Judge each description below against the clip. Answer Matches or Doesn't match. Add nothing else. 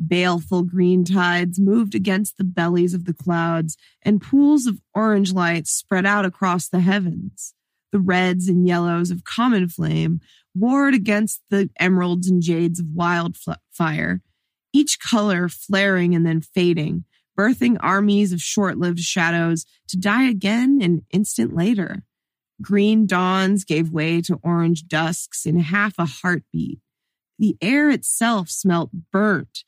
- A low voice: Doesn't match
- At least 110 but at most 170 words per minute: Matches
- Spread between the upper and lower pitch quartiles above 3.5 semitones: Doesn't match